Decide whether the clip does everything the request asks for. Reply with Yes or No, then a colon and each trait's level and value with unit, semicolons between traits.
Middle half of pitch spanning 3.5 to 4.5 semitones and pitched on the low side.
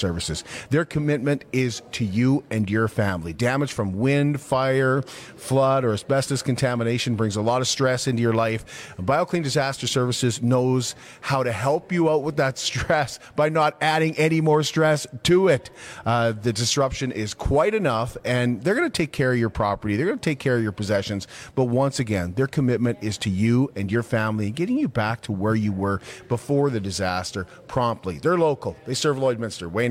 Yes: average, 4.1 semitones; low, 125 Hz